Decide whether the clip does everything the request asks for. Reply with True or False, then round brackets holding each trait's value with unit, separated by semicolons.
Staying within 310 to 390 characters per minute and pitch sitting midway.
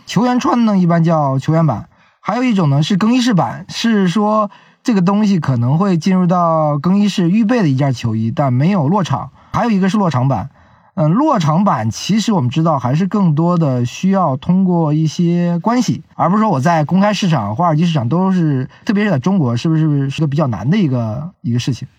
True (320 characters per minute; 170 Hz)